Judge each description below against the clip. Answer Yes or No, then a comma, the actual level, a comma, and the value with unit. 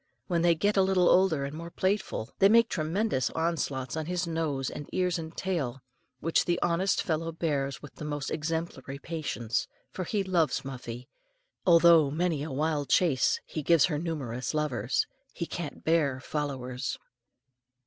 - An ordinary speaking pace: Yes, average, 160 wpm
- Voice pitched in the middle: Yes, medium, 160 Hz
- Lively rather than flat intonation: No, average, 3.7 semitones